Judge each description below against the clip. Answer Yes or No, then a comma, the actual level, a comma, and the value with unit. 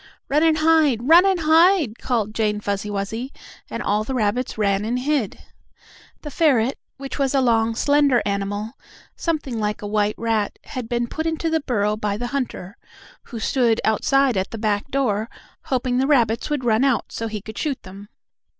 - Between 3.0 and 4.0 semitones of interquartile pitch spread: No, average, 4.7 semitones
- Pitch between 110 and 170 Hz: No, high, 235 Hz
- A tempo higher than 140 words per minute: Yes, average, 185 wpm